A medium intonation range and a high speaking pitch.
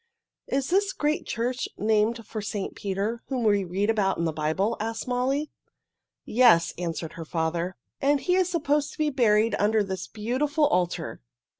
No: wide, 6.0 semitones; high, 220 Hz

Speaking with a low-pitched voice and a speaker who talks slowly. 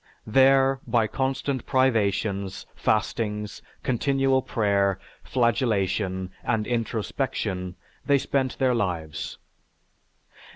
Yes: low, 115 Hz; slow, 80 wpm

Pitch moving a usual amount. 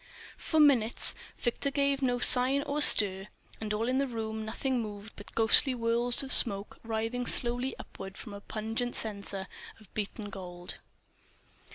Yes: average, 3.3 semitones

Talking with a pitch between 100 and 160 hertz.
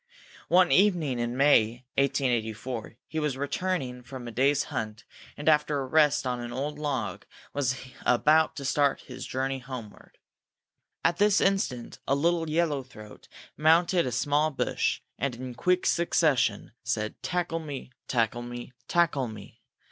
Yes: low, 135 Hz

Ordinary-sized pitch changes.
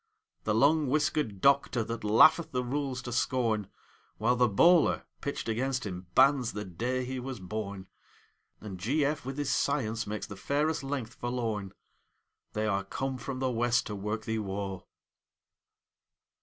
Yes: average, 4.3 semitones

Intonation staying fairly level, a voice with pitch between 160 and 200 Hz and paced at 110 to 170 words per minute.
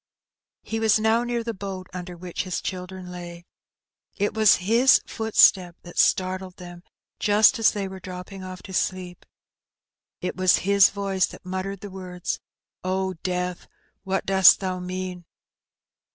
Yes: narrow, 1.8 semitones; medium, 185 Hz; average, 150 wpm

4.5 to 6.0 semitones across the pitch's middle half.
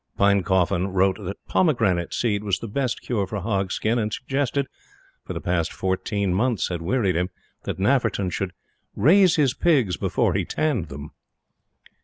Yes: average, 5.1 semitones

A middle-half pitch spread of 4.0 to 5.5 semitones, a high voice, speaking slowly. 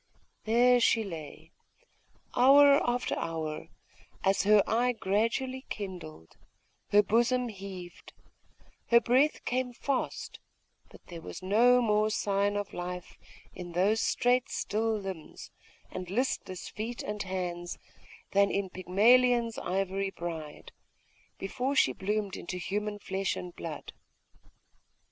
Yes: average, 4.7 semitones; high, 205 Hz; slow, 115 wpm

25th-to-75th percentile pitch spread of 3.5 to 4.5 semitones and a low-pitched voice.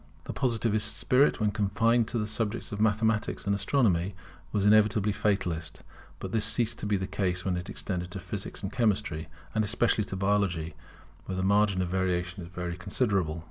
No: average, 2.9 semitones; low, 100 Hz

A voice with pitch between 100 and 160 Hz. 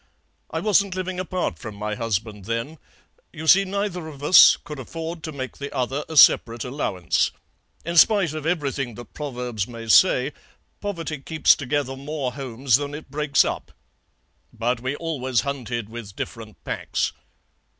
Yes: medium, 140 Hz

